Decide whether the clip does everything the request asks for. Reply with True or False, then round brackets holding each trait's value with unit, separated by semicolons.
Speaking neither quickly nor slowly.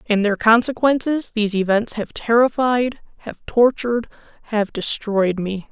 False (105 wpm)